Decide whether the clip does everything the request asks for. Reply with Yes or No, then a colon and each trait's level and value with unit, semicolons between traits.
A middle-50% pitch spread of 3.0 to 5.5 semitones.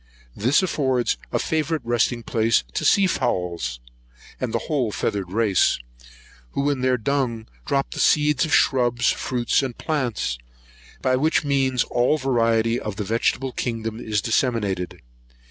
Yes: average, 3.6 semitones